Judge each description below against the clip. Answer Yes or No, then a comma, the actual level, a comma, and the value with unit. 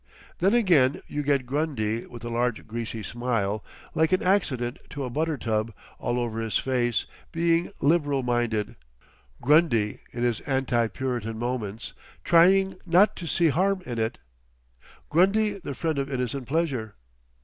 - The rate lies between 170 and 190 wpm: No, slow, 135 wpm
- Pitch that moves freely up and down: Yes, wide, 6.2 semitones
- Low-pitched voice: Yes, low, 125 Hz